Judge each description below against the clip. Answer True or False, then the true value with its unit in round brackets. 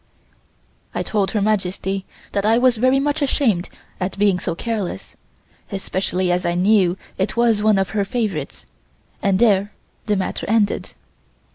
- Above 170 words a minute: False (150 wpm)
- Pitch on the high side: True (200 Hz)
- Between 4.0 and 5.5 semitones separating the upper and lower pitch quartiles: False (2.9 semitones)